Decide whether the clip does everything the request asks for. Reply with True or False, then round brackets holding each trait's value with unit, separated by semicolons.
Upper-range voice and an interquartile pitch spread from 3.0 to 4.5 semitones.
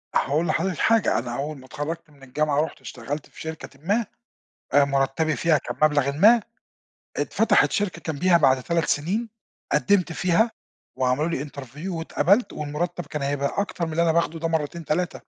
False (155 Hz; 3.3 semitones)